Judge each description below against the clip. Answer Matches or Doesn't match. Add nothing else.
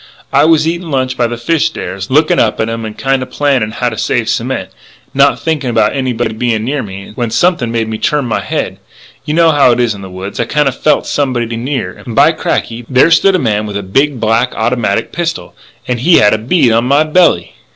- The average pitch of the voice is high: Doesn't match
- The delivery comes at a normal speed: Doesn't match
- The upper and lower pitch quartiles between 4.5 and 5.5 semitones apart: Matches